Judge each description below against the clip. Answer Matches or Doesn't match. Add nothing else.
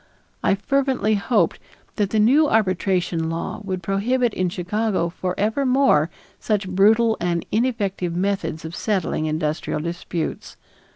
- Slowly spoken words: Matches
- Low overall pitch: Doesn't match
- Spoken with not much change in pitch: Doesn't match